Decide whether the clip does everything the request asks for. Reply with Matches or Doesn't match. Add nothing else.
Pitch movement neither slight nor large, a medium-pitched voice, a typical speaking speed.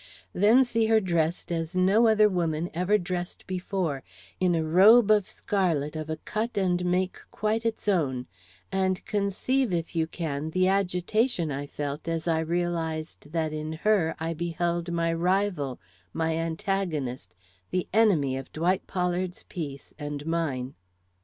Matches